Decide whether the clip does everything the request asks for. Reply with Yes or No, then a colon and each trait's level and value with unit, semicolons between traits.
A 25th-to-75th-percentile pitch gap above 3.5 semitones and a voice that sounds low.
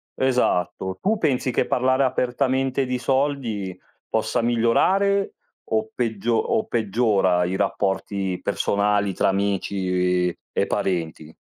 Yes: wide, 5.4 semitones; low, 110 Hz